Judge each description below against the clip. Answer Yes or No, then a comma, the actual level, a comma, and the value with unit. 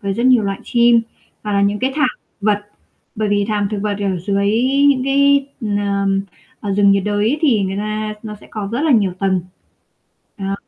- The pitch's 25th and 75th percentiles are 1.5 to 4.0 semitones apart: Yes, average, 2.9 semitones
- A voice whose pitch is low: No, high, 205 Hz